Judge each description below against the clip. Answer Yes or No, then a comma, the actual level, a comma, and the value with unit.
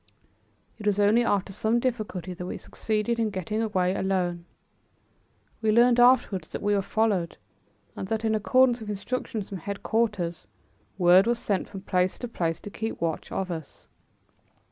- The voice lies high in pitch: Yes, high, 205 Hz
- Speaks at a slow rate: No, average, 165 wpm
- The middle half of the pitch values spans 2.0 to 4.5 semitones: Yes, average, 3.4 semitones